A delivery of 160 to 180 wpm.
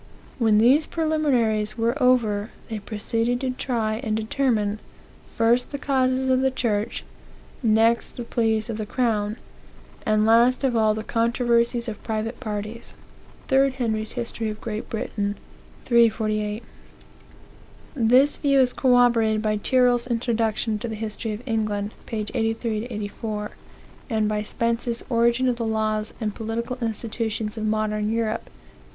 No: average, 140 wpm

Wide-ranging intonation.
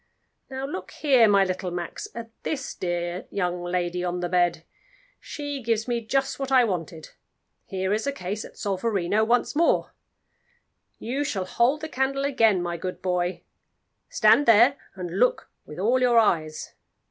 Yes: wide, 6.2 semitones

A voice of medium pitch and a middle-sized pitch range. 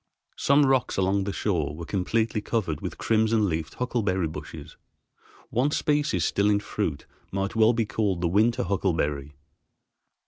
No: low, 100 Hz; average, 4.7 semitones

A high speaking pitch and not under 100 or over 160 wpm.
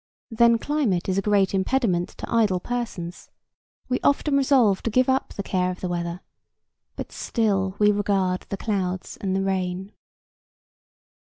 Yes: high, 195 Hz; average, 155 wpm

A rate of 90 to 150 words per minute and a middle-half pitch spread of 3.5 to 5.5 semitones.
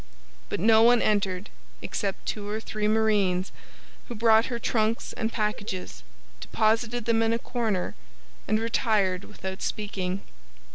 No: slow, 135 wpm; narrow, 2.6 semitones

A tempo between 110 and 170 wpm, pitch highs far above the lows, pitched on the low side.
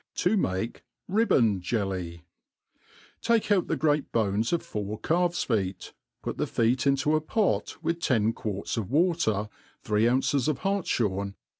Yes: average, 145 wpm; wide, 8.3 semitones; low, 120 Hz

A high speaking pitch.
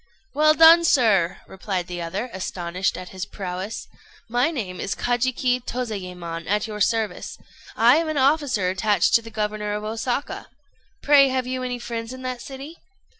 Yes: high, 225 Hz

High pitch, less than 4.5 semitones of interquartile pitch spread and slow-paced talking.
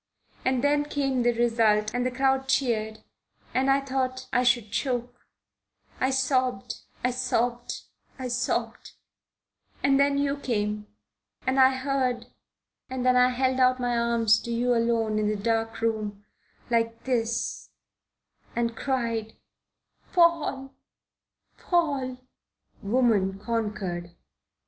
Yes: high, 245 Hz; narrow, 2.5 semitones; slow, 120 wpm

